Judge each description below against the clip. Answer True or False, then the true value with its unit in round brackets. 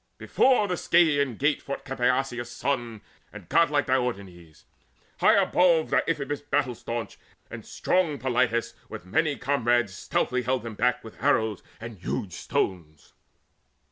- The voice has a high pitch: False (125 Hz)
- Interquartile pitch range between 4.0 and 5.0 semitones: True (4.5 semitones)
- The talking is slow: True (130 wpm)